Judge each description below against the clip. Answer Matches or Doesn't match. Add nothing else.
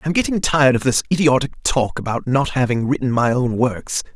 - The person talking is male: Matches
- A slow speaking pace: Doesn't match